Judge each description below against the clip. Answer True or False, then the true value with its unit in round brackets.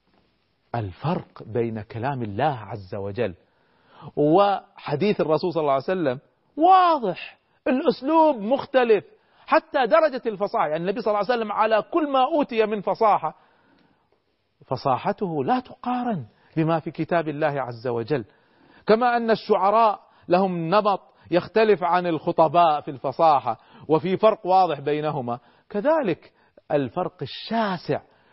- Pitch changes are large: True (7.2 semitones)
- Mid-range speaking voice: True (180 Hz)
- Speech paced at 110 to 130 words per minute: True (120 wpm)